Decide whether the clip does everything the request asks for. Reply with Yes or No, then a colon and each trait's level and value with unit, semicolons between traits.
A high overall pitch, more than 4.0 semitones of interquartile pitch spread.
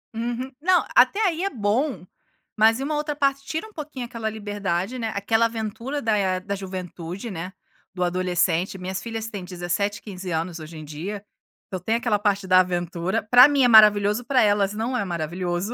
Yes: high, 205 Hz; average, 4.6 semitones